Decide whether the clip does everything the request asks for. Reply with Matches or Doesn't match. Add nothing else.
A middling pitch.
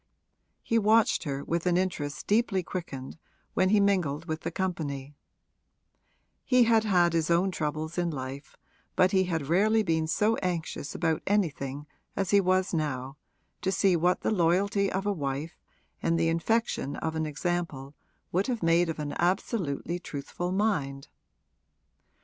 Matches